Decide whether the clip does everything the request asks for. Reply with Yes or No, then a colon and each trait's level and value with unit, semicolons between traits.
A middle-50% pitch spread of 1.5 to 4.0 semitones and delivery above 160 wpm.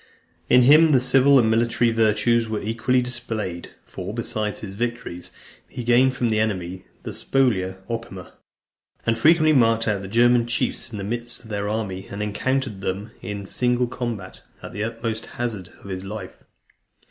Yes: average, 2.9 semitones; average, 170 wpm